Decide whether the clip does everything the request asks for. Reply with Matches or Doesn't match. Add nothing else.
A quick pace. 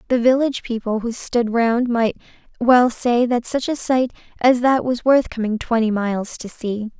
Doesn't match